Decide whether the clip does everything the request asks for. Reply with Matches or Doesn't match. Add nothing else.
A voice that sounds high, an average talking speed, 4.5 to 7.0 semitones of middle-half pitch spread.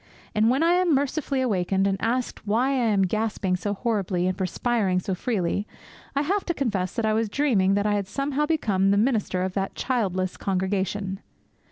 Matches